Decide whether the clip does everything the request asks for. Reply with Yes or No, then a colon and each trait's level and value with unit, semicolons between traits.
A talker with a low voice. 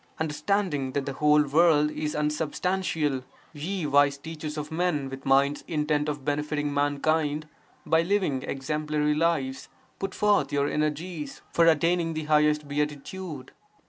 No: medium, 150 Hz